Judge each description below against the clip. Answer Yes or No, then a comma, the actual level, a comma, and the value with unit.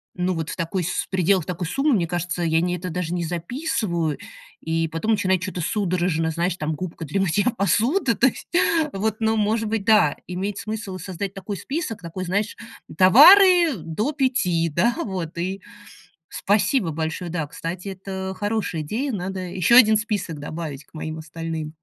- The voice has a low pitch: No, medium, 185 Hz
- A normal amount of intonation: Yes, average, 4.4 semitones